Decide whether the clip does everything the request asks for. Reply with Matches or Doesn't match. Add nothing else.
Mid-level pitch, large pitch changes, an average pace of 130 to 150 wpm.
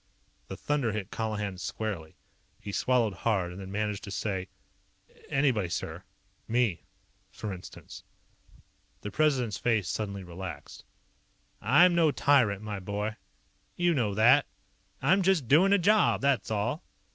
Doesn't match